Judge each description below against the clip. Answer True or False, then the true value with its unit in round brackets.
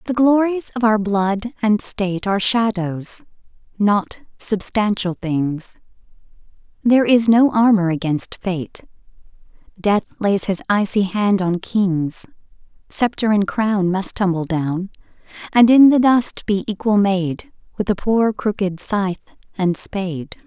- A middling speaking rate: False (130 wpm)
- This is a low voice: False (200 Hz)